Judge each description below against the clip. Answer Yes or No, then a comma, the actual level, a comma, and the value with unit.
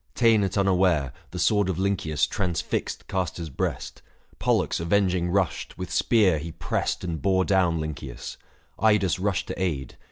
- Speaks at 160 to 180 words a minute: No, average, 150 wpm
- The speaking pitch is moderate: No, very low, 90 Hz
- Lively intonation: No, average, 2.9 semitones